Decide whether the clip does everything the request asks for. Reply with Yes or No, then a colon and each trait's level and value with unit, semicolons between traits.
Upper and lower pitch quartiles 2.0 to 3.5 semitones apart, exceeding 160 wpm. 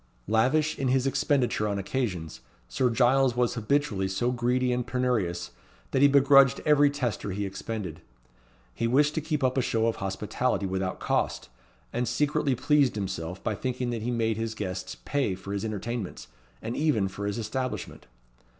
No: average, 4.7 semitones; average, 170 wpm